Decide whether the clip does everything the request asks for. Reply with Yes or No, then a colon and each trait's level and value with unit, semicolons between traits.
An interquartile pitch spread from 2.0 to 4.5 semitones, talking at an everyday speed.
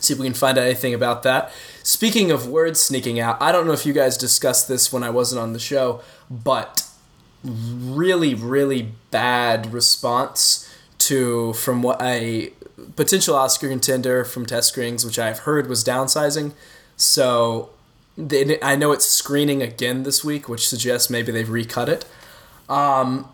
Yes: average, 2.7 semitones; average, 165 wpm